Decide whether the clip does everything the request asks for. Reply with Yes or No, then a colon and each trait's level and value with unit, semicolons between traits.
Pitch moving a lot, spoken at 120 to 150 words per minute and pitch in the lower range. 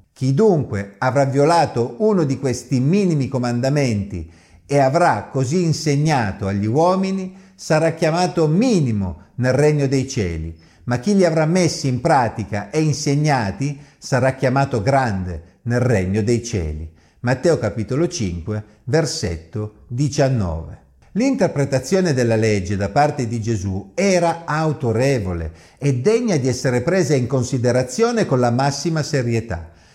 Yes: wide, 6.6 semitones; average, 125 wpm; low, 130 Hz